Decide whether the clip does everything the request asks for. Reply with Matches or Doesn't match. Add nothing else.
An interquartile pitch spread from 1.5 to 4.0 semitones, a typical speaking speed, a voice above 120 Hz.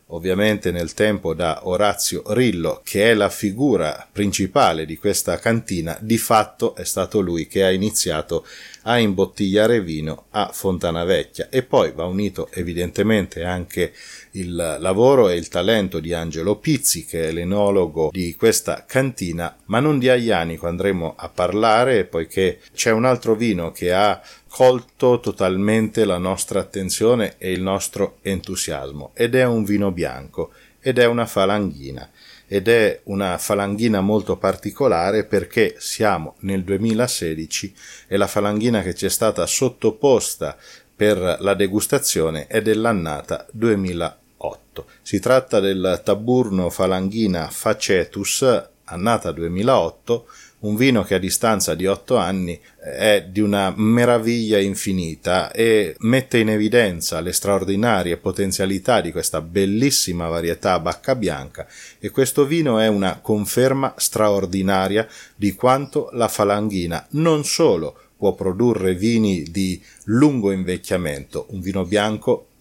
Doesn't match